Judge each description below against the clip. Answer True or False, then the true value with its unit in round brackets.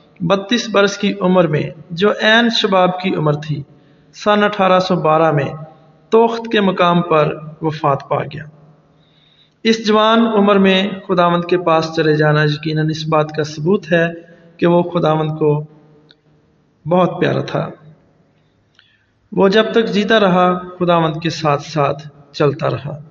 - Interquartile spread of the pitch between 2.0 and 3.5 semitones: False (3.9 semitones)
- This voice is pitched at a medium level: True (165 Hz)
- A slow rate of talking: False (145 wpm)